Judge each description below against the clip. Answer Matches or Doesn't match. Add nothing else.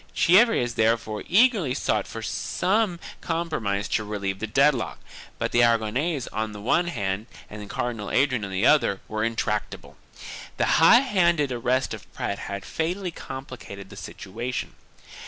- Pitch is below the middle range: Matches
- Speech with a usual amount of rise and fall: Doesn't match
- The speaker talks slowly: Doesn't match